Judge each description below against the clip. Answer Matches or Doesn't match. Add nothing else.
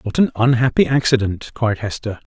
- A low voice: Matches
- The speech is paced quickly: Doesn't match